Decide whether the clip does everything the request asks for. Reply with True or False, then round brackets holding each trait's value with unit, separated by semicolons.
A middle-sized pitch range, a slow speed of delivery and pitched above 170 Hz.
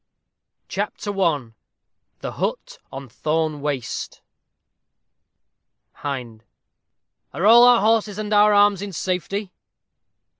False (6.2 semitones; 100 wpm; 190 Hz)